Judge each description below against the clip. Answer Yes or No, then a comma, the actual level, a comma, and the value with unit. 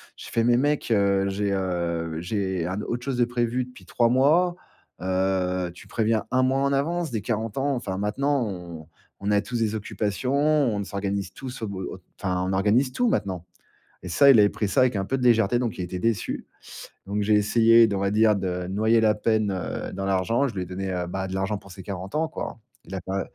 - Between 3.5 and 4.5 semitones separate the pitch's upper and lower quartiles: Yes, average, 4.2 semitones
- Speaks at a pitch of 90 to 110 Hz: Yes, low, 105 Hz